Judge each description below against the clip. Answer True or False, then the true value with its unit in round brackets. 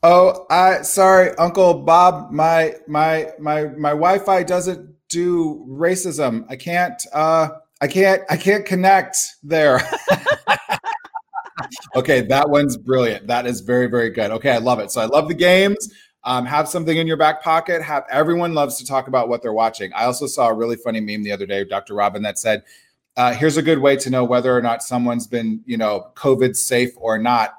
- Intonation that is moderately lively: False (6.3 semitones)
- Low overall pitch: False (155 Hz)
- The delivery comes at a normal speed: True (190 wpm)